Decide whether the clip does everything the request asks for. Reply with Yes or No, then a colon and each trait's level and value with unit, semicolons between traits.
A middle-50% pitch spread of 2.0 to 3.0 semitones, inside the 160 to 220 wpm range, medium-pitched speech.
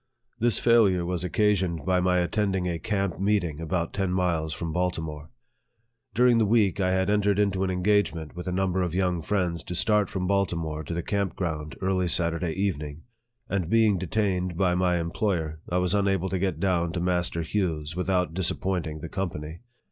No: average, 2.7 semitones; average, 180 wpm; very low, 90 Hz